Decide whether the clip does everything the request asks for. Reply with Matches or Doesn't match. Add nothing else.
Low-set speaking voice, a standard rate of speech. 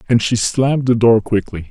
Doesn't match